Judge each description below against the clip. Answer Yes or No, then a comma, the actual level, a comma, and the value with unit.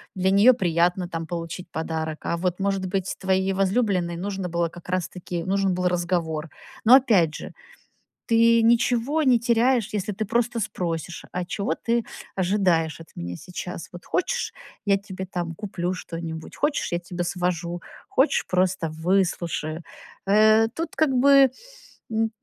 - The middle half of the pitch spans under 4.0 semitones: No, average, 4.3 semitones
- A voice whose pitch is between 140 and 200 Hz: Yes, medium, 185 Hz